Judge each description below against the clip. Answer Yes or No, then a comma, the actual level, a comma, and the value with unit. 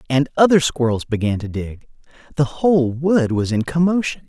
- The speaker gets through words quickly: No, average, 155 wpm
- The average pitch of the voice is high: No, medium, 140 Hz